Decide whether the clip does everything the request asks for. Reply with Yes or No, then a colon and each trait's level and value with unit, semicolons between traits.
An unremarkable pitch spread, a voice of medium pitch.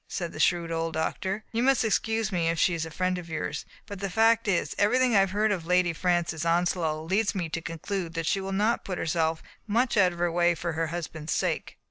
Yes: average, 3.5 semitones; medium, 180 Hz